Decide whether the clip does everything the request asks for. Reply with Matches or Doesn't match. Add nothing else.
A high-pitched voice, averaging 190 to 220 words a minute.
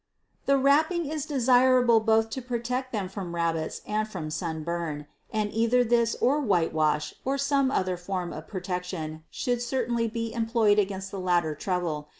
Doesn't match